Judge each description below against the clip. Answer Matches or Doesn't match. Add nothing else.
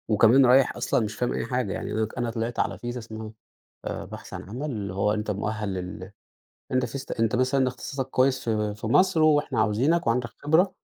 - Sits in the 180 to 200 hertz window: Doesn't match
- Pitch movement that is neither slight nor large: Matches